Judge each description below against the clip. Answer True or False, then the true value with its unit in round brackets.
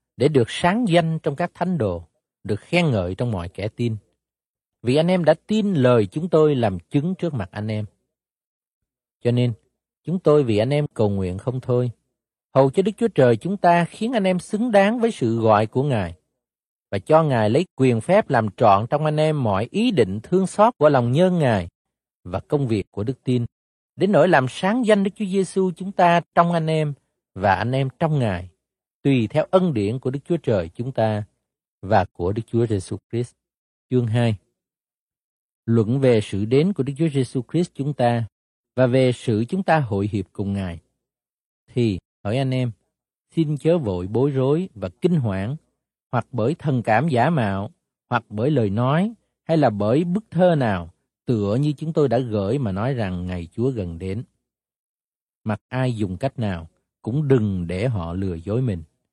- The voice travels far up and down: True (6.8 semitones)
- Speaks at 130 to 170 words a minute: False (195 wpm)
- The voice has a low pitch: True (125 Hz)